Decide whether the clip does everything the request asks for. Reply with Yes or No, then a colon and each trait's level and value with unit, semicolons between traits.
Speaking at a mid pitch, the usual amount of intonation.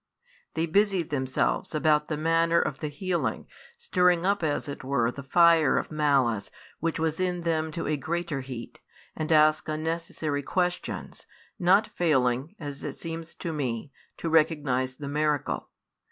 Yes: medium, 155 Hz; average, 3.0 semitones